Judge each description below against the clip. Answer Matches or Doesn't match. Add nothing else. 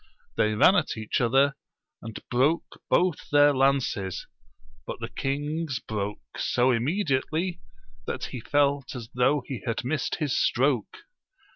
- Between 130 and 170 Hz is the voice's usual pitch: Matches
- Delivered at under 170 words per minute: Matches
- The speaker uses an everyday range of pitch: Matches